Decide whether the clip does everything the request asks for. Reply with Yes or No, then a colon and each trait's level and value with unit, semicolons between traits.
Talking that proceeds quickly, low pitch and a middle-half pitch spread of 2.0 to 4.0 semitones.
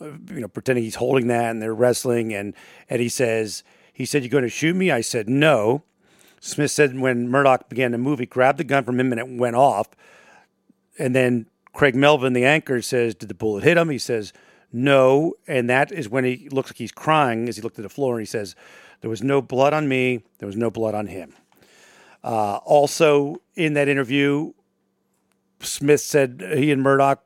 Yes: fast, 210 wpm; low, 130 Hz; average, 3.3 semitones